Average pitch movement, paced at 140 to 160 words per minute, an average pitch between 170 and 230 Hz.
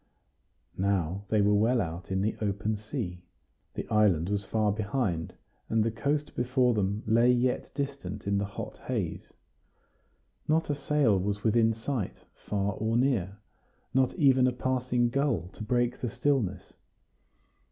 No: average, 4.0 semitones; average, 150 wpm; low, 110 Hz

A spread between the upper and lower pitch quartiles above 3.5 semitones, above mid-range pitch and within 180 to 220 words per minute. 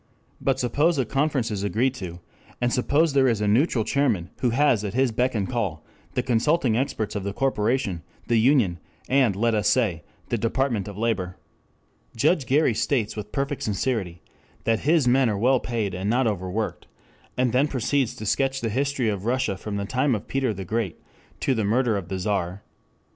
No: average, 4.4 semitones; low, 115 Hz; average, 195 wpm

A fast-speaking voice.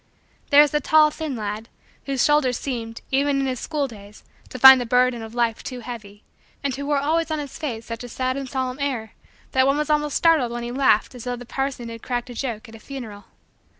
Yes: fast, 235 wpm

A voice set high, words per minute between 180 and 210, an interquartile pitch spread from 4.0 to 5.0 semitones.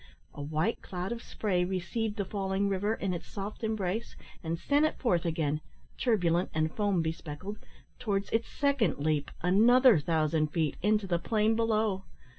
No: high, 195 Hz; average, 160 wpm; average, 4.7 semitones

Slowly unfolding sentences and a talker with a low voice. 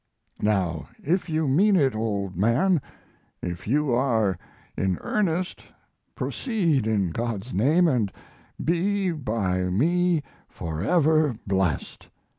Yes: slow, 105 wpm; low, 125 Hz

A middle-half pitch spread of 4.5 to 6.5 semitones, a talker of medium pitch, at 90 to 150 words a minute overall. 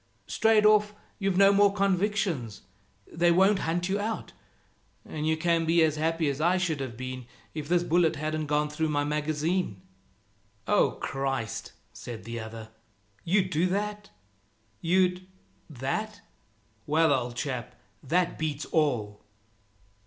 Yes: average, 4.8 semitones; medium, 160 Hz; average, 140 wpm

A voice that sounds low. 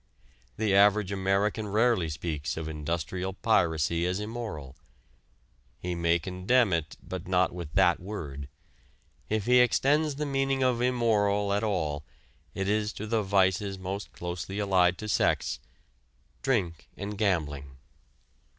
Yes: very low, 95 Hz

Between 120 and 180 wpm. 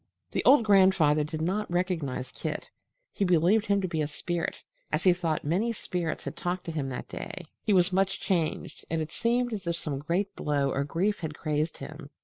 No: average, 195 wpm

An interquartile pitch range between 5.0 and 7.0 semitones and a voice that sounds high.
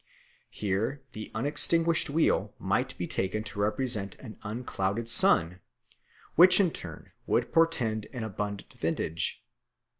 No: wide, 5.6 semitones; low, 110 Hz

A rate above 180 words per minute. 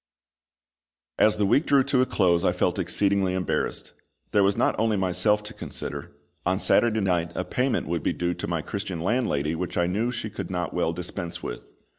Yes: average, 195 wpm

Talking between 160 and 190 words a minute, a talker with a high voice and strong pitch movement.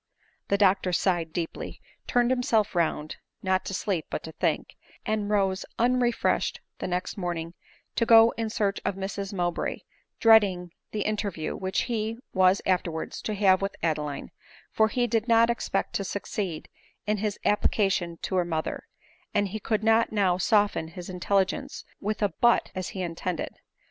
No: average, 165 wpm; high, 195 Hz; average, 3.3 semitones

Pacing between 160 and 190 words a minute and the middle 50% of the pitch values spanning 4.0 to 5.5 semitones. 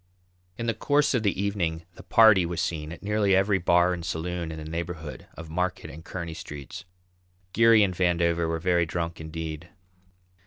No: average, 180 wpm; average, 2.9 semitones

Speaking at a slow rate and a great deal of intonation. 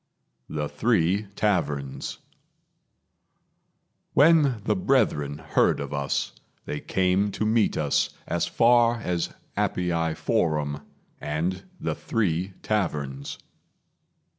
Yes: slow, 95 wpm; wide, 6.4 semitones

